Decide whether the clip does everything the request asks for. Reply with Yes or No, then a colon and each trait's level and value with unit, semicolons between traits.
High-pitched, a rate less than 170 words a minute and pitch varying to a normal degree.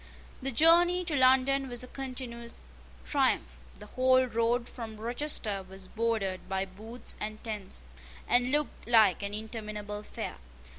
Yes: high, 230 Hz; average, 140 wpm; average, 3.6 semitones